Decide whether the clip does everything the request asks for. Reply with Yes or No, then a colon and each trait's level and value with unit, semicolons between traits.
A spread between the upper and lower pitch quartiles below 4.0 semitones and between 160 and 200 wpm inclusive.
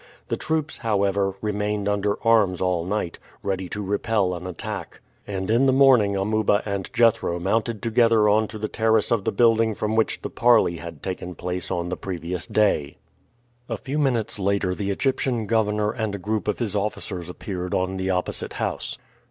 Yes: average, 3.1 semitones; average, 180 wpm